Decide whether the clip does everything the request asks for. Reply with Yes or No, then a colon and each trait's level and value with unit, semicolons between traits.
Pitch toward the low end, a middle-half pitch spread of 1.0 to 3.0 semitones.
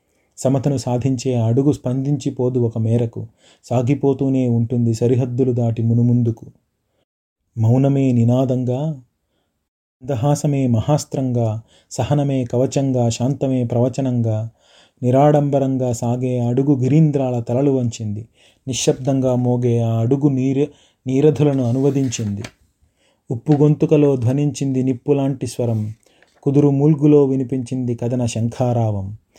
Yes: low, 130 Hz; narrow, 2.6 semitones